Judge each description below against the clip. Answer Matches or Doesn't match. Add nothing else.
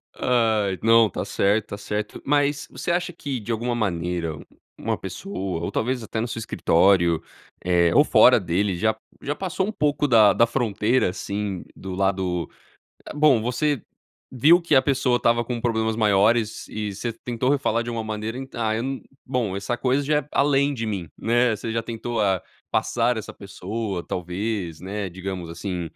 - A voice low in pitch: Matches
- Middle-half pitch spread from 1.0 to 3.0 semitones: Doesn't match